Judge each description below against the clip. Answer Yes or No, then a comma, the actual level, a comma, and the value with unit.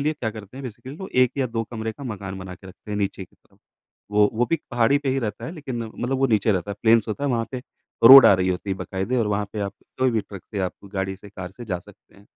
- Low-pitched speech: Yes, low, 110 Hz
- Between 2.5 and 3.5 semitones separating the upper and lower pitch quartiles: No, average, 4.1 semitones